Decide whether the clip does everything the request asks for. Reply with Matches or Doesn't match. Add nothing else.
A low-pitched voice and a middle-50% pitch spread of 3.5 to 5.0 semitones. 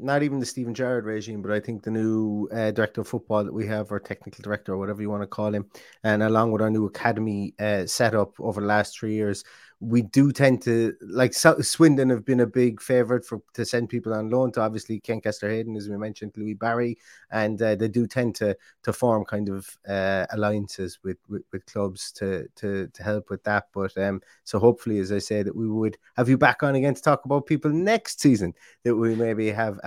Doesn't match